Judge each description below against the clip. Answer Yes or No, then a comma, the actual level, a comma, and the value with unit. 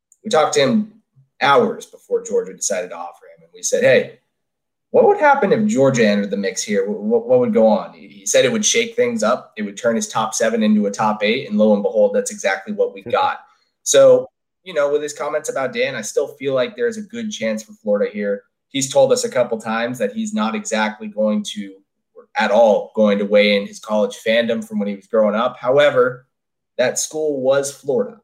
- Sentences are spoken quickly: Yes, fast, 225 wpm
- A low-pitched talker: No, medium, 155 Hz